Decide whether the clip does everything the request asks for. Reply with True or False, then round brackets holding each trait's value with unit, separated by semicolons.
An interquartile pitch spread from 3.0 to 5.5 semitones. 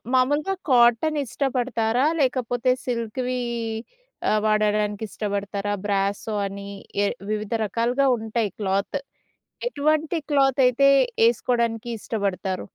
True (3.7 semitones)